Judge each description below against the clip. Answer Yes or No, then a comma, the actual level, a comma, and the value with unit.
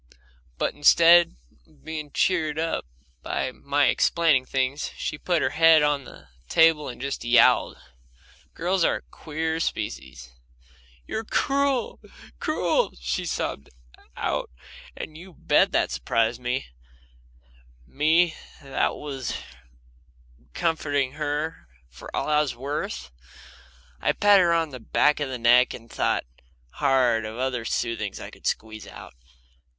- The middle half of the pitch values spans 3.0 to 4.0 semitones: No, average, 4.8 semitones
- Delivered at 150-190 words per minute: No, slow, 135 wpm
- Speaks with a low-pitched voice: No, medium, 145 Hz